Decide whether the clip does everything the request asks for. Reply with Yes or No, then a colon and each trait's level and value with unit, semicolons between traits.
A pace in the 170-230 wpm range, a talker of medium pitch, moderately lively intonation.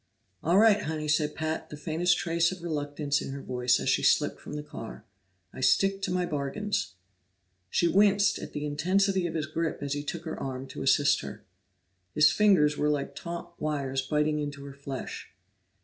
Yes: average, 190 wpm; medium, 150 Hz; average, 3.5 semitones